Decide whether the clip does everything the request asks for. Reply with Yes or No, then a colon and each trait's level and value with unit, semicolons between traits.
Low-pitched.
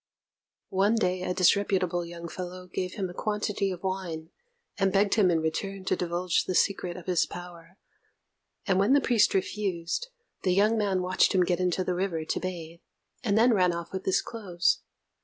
No: medium, 185 Hz